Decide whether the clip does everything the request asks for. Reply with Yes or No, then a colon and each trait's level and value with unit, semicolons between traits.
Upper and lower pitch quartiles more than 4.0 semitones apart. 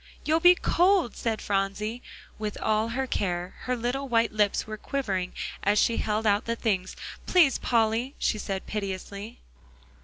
No: average, 3.5 semitones